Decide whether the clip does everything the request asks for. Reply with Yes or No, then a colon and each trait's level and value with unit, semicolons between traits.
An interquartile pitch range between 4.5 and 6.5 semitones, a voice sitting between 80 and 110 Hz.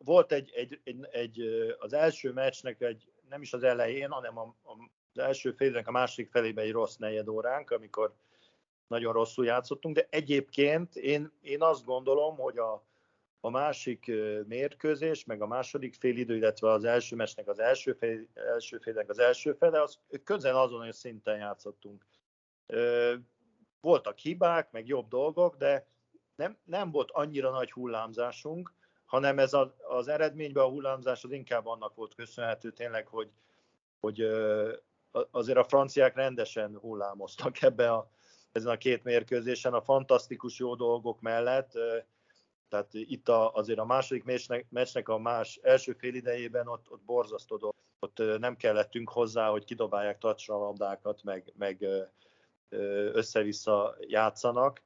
No: average, 5.0 semitones; low, 125 Hz